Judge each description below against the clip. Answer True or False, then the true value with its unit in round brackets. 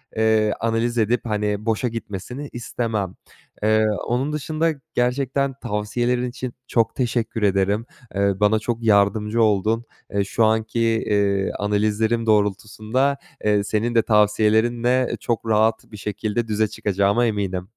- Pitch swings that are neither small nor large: False (2.3 semitones)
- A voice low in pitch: True (110 Hz)